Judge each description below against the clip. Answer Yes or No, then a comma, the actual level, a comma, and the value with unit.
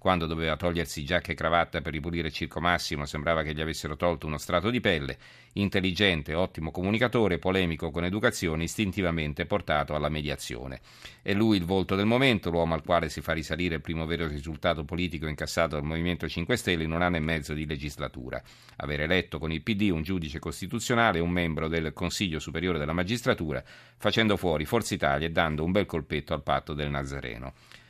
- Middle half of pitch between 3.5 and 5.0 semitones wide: No, average, 3.0 semitones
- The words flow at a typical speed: No, fast, 185 wpm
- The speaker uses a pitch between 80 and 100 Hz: Yes, very low, 85 Hz